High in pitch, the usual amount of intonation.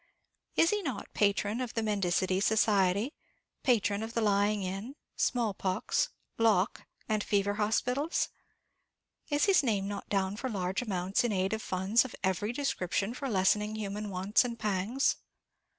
Yes: high, 210 Hz; average, 3.2 semitones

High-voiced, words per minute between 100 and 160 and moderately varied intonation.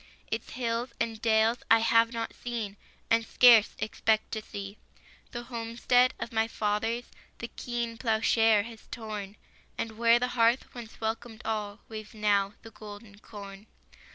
No: high, 225 Hz; average, 150 wpm; narrow, 1.5 semitones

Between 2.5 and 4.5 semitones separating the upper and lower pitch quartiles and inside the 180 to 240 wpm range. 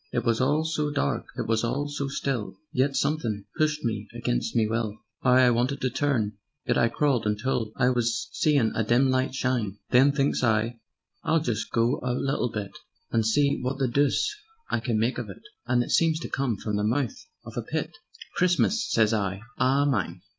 Yes: average, 3.9 semitones; average, 200 wpm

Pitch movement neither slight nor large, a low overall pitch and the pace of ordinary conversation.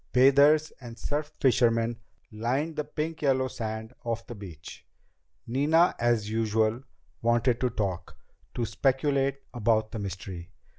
No: average, 3.8 semitones; low, 120 Hz; slow, 130 wpm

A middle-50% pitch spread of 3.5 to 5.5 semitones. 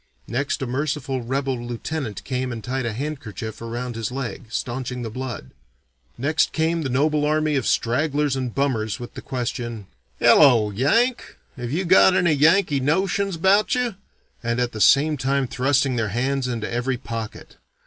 Yes: average, 3.9 semitones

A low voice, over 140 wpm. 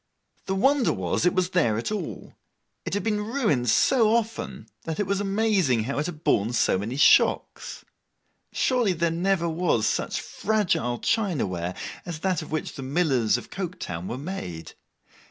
No: medium, 170 Hz; average, 170 wpm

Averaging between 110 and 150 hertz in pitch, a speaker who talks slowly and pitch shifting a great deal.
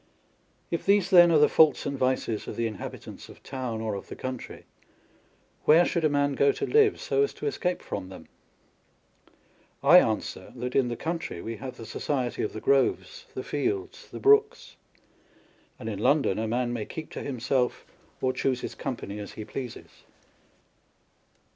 No: low, 135 Hz; average, 180 wpm; wide, 6.5 semitones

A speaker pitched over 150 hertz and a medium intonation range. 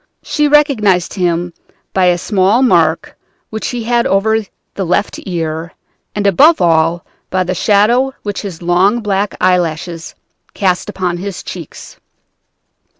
Yes: high, 190 Hz; average, 3.7 semitones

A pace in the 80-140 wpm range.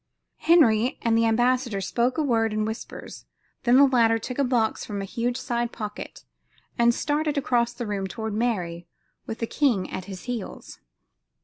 No: average, 175 wpm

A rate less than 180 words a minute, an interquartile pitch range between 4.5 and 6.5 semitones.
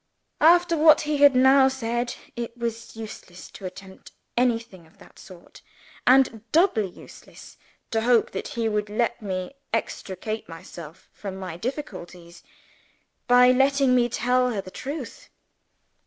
Yes: average, 140 wpm; average, 5.3 semitones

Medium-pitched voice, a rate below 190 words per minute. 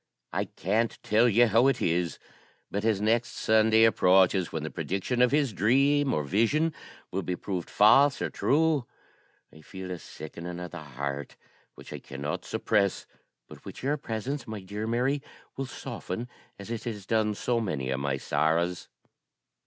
No: low, 105 Hz; average, 170 wpm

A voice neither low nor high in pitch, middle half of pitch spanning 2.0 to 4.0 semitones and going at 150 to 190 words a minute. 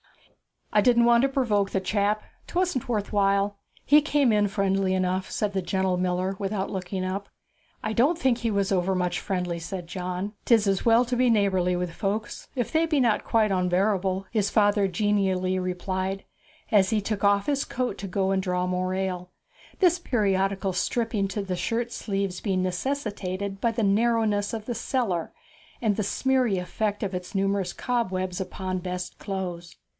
No: high, 195 Hz; average, 3.0 semitones; average, 175 wpm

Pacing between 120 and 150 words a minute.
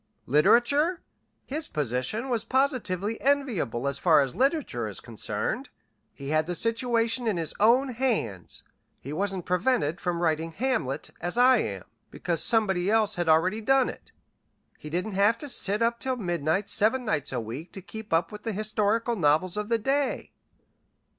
No: average, 165 wpm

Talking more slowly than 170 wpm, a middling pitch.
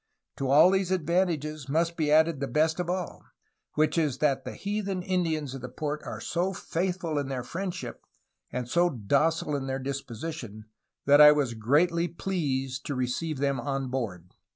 No: average, 175 wpm; medium, 150 Hz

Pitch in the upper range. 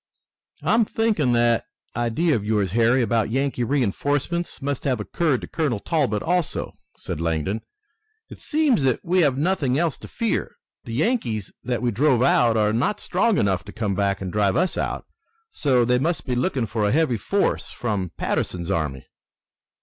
No: low, 125 Hz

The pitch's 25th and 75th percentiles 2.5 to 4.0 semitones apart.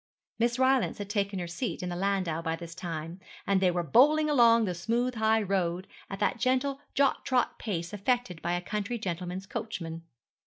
No: average, 5.2 semitones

